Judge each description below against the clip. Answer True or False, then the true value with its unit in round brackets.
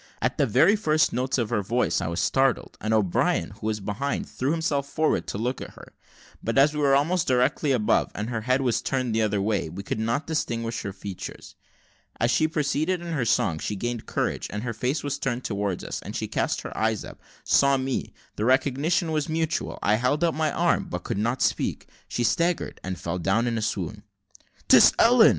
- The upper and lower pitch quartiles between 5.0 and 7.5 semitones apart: True (5.5 semitones)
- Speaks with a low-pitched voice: True (125 Hz)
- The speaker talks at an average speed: False (215 wpm)